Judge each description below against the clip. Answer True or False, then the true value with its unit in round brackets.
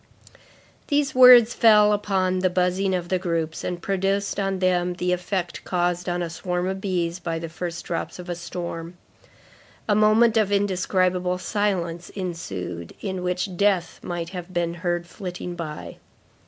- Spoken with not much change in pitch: True (2.1 semitones)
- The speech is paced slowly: False (155 wpm)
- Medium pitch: True (180 Hz)